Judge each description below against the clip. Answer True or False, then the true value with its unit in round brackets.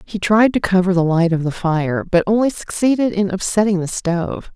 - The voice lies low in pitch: False (190 Hz)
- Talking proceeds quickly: True (210 wpm)